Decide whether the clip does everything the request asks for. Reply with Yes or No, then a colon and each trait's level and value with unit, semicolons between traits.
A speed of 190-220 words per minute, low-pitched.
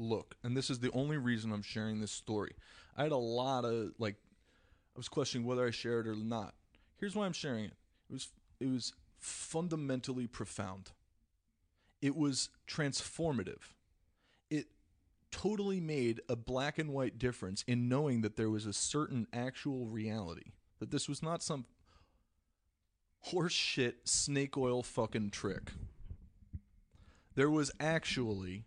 No: average, 150 wpm; low, 115 Hz